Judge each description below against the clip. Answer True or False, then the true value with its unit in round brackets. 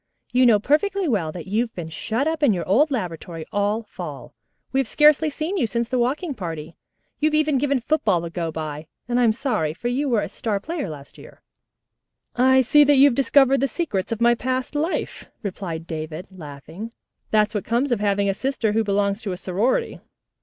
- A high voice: True (230 Hz)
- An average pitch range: False (6.7 semitones)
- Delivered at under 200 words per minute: False (205 wpm)